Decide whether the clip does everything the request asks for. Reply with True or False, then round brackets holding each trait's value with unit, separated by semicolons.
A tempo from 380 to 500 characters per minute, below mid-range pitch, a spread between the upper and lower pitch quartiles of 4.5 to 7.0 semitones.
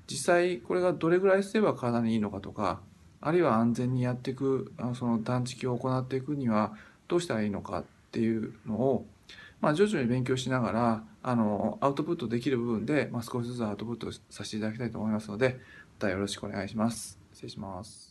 False (435 characters per minute; 115 Hz; 3.4 semitones)